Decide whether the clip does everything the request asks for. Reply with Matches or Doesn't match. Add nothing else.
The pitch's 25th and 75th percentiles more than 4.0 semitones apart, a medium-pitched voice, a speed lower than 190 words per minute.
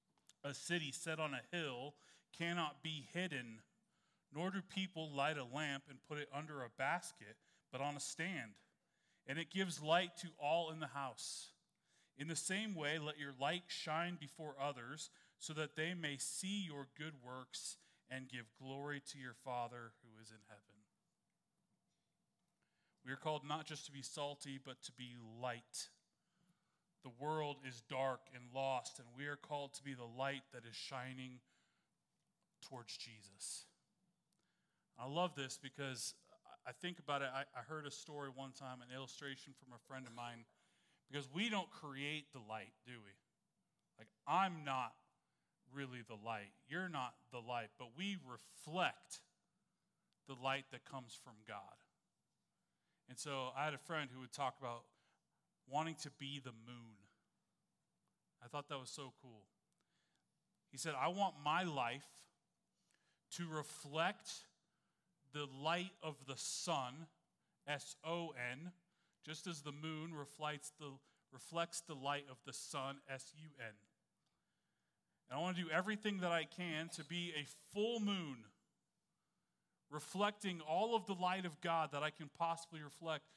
Matches